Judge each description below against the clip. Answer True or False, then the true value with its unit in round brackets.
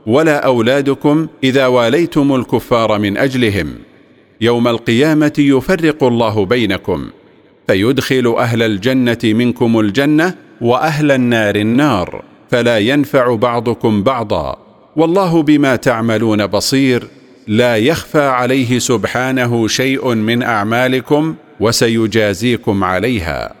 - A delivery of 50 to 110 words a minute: True (95 wpm)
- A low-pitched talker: True (125 Hz)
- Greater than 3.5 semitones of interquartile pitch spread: False (3.2 semitones)